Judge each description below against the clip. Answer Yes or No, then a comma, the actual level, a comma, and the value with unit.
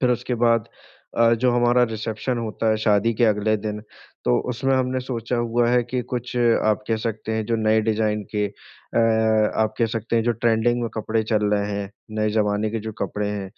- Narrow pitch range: Yes, narrow, 1.9 semitones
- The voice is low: Yes, low, 110 Hz